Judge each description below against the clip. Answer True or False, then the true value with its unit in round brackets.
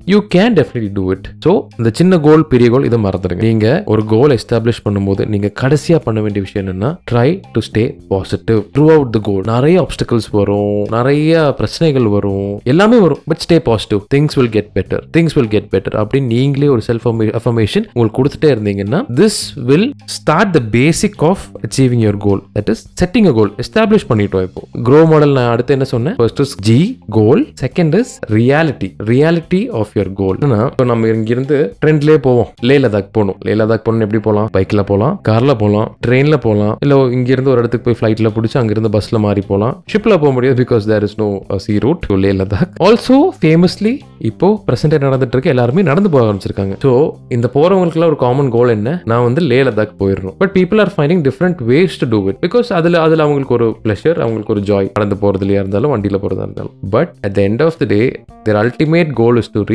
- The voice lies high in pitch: False (120 Hz)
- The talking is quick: True (145 wpm)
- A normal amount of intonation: False (6.4 semitones)